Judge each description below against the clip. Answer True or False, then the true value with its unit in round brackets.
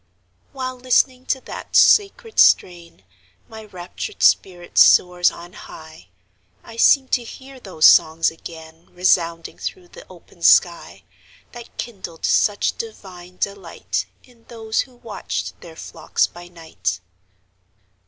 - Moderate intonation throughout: False (6.4 semitones)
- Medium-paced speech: False (125 wpm)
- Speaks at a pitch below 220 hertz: True (190 Hz)